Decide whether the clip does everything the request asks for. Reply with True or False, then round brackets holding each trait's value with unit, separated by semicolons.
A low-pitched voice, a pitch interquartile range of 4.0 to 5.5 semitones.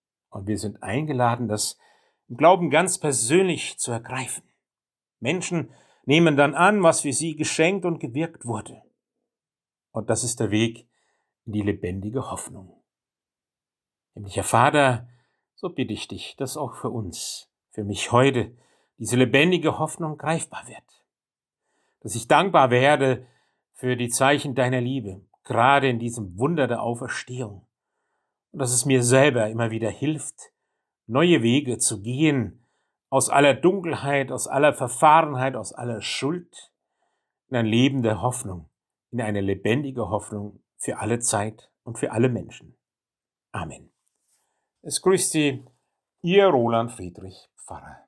True (125 Hz; 4.6 semitones)